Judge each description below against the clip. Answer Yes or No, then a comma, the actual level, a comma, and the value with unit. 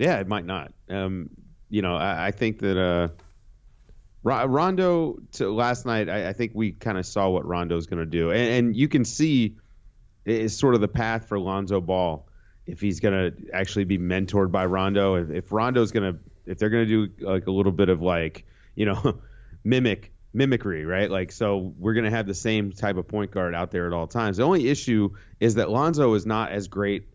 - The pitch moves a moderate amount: Yes, average, 3.4 semitones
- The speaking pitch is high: No, low, 100 Hz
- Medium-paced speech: No, fast, 220 wpm